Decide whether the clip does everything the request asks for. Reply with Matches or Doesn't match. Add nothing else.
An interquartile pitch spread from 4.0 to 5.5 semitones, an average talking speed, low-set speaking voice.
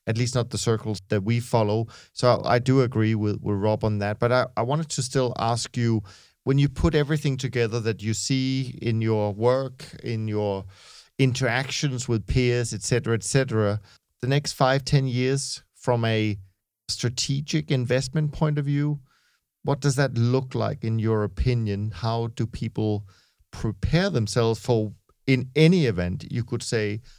Doesn't match